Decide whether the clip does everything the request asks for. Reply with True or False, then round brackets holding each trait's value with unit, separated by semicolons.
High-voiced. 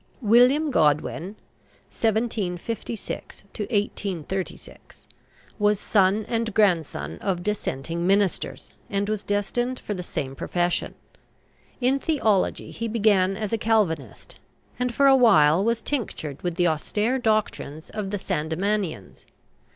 True (205 Hz)